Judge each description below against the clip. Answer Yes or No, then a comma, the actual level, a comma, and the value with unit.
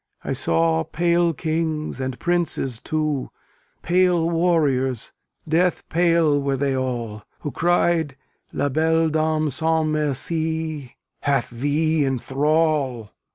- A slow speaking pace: Yes, slow, 110 wpm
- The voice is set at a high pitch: No, medium, 155 Hz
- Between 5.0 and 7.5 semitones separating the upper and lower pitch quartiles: No, average, 3.5 semitones